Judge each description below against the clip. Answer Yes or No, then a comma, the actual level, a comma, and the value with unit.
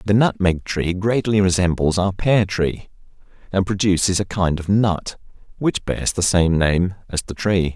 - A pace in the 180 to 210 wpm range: No, average, 170 wpm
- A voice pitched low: Yes, very low, 95 Hz